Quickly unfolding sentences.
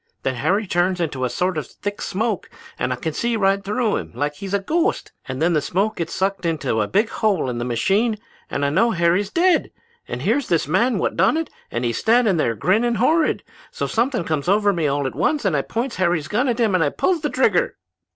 Yes: fast, 235 wpm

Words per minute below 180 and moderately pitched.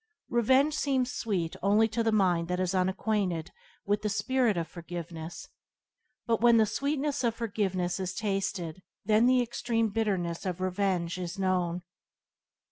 No: average, 145 wpm; high, 200 Hz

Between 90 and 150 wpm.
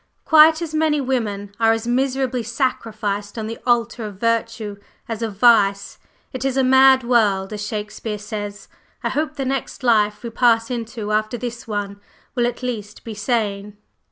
No: average, 170 wpm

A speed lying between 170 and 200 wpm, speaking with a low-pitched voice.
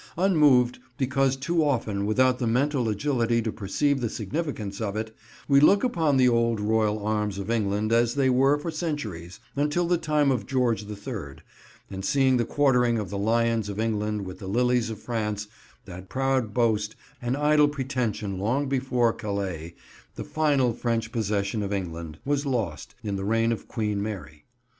Yes: average, 175 wpm; low, 115 Hz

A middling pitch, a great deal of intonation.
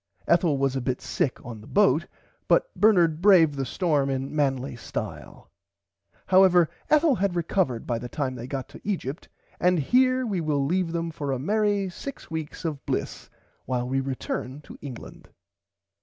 Yes: medium, 155 Hz; wide, 5.8 semitones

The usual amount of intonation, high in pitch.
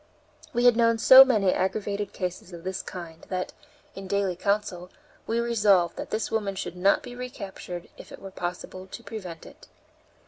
Yes: average, 3.6 semitones; high, 195 Hz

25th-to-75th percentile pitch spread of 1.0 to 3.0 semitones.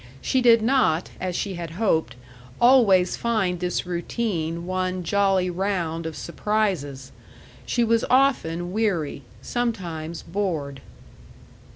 No: average, 4.7 semitones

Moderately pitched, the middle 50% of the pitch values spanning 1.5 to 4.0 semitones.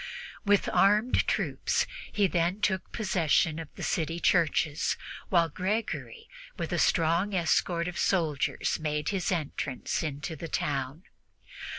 Yes: medium, 170 Hz; average, 3.5 semitones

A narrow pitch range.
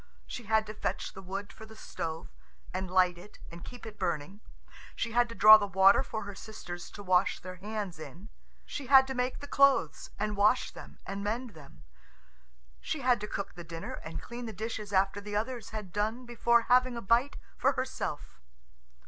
No: average, 3.9 semitones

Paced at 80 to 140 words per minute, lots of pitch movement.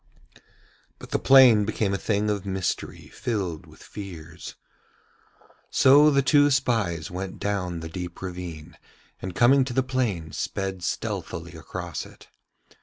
Yes: slow, 135 wpm; wide, 5.8 semitones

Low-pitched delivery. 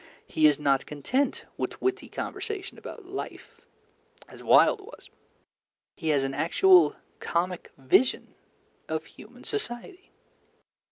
No: medium, 185 Hz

